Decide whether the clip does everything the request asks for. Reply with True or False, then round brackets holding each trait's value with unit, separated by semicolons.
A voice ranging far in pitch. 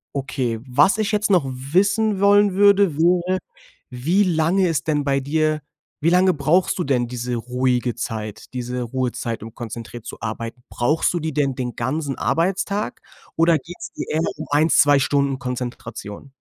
True (6.0 semitones)